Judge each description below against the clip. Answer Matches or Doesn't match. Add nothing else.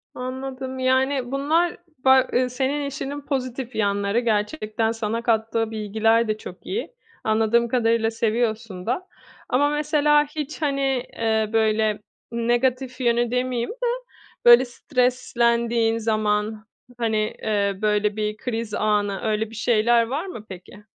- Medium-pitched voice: Doesn't match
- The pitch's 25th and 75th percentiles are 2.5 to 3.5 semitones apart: Matches